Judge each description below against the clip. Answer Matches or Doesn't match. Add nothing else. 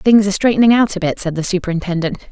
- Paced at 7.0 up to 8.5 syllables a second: Matches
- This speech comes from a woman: Matches